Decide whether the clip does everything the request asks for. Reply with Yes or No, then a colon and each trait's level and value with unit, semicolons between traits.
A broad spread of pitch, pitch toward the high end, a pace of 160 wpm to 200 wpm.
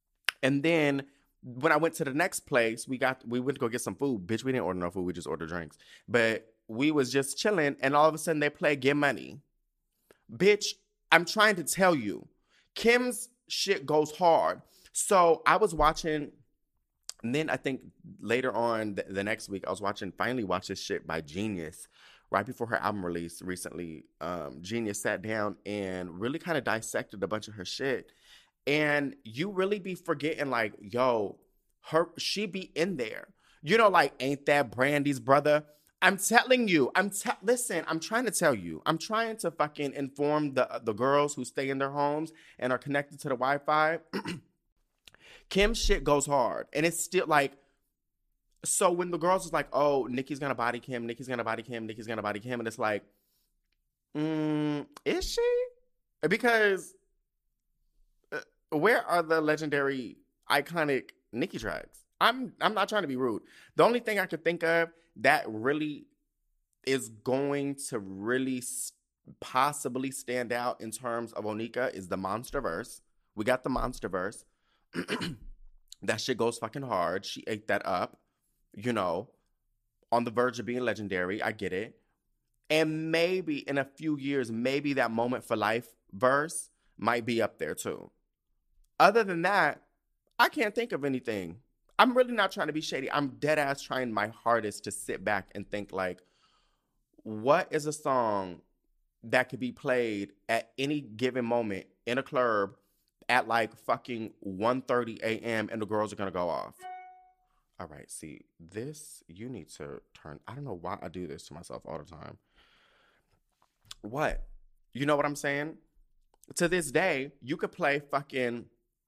No: wide, 6.2 semitones; low, 135 Hz; average, 175 wpm